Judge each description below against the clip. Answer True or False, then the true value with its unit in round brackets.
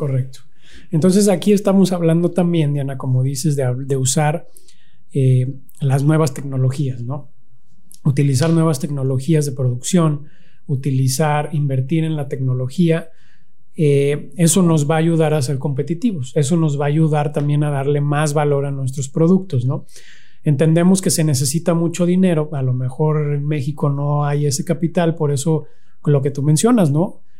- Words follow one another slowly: False (160 wpm)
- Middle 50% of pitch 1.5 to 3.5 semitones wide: True (2.8 semitones)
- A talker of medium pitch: True (150 Hz)